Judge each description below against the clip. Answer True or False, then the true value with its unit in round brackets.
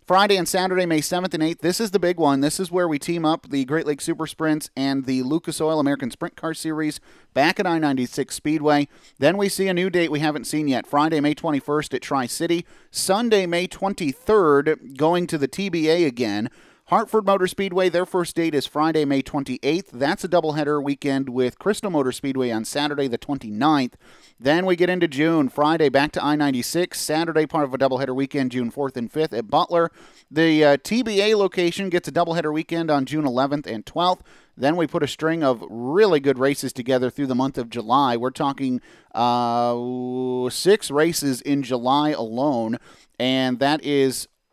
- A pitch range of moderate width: True (4.0 semitones)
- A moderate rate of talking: True (190 wpm)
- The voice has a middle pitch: True (150 Hz)